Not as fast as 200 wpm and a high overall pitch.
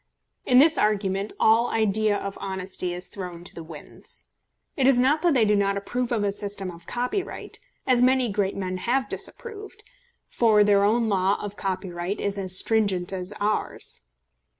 Yes: average, 175 wpm; high, 205 Hz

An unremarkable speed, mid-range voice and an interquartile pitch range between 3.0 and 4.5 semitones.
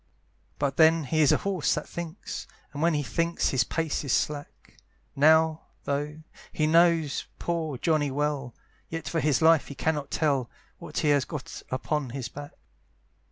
No: average, 165 wpm; medium, 150 Hz; narrow, 2.4 semitones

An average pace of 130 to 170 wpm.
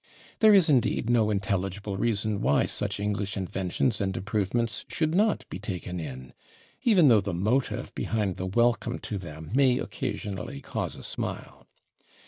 Yes: average, 150 wpm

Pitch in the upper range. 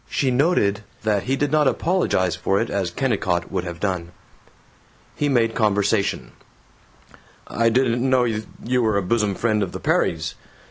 No: low, 110 Hz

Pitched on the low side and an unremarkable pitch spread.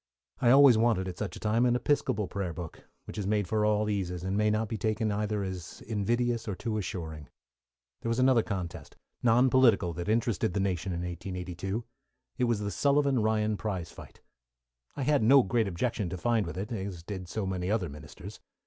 Yes: low, 105 Hz; average, 3.9 semitones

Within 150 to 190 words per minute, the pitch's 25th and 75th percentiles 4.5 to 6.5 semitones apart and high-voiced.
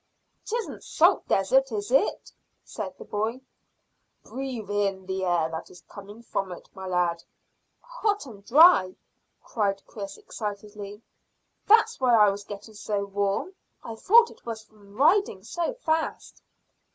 No: average, 140 wpm; wide, 5.4 semitones; high, 210 Hz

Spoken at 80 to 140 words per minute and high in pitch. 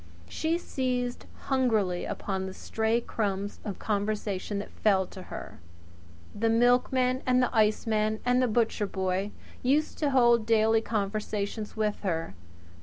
Yes: slow, 135 wpm; high, 220 Hz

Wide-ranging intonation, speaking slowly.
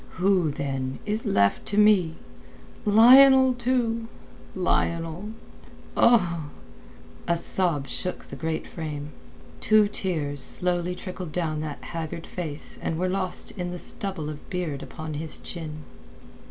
No: average, 4.5 semitones; slow, 125 wpm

